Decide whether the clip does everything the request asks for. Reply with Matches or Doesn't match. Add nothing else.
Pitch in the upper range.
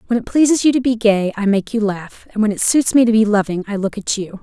Matches